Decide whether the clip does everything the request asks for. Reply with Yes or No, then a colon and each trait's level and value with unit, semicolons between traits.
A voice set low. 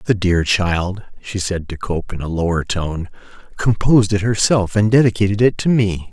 Yes: low, 100 Hz